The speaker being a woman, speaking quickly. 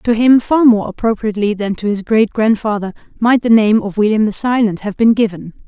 Yes: female; fast, 210 wpm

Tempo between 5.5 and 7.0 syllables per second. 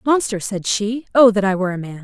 Yes: 6.0 syllables/s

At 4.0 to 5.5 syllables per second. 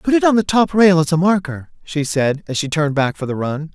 No: 5.7 syllables/s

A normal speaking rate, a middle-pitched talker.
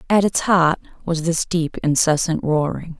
Yes: average, 160 wpm; medium, 165 Hz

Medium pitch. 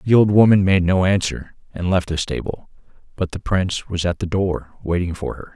No: very low, 90 Hz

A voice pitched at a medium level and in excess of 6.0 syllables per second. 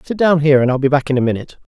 Yes: medium, 145 Hz; 8.5 syllables/s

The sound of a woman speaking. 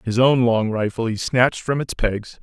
No: male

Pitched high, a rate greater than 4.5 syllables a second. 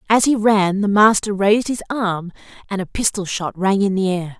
Yes: high, 200 Hz; 5.1 syllables/s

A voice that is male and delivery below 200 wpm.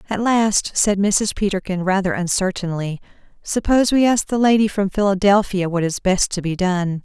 No: female; average, 170 wpm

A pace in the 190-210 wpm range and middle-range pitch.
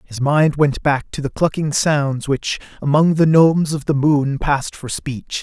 Yes: average, 200 wpm; medium, 145 Hz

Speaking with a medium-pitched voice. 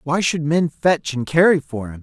Yes: medium, 150 Hz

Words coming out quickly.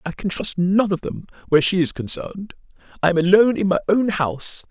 Yes: fast, 215 wpm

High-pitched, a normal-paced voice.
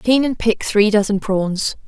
Yes: high, 215 Hz; average, 190 wpm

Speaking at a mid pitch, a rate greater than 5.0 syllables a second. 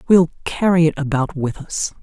No: medium, 160 Hz; 4.9 syllables/s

